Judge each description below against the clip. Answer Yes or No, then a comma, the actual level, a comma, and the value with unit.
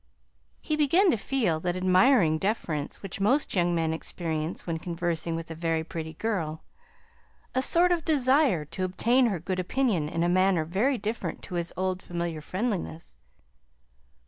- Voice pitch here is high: No, medium, 180 Hz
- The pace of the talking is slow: No, average, 160 wpm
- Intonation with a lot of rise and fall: Yes, wide, 6.1 semitones